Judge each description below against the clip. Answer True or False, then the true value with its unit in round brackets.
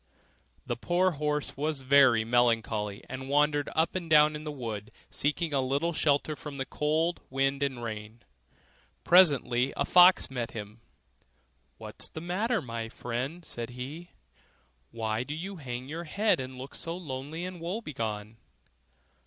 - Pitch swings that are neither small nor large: True (4.9 semitones)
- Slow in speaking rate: False (155 wpm)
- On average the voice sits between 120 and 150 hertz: True (140 Hz)